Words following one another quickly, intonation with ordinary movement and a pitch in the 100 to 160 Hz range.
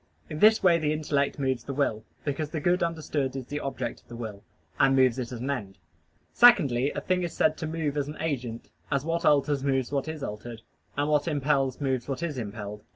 Yes: fast, 220 wpm; average, 3.4 semitones; medium, 140 Hz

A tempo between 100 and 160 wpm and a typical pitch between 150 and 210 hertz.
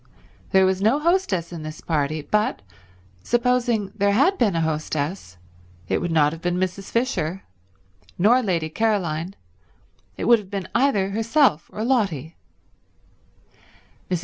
Yes: average, 140 wpm; high, 190 Hz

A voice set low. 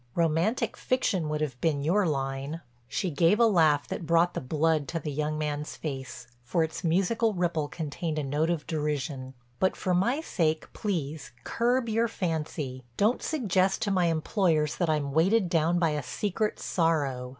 No: medium, 160 Hz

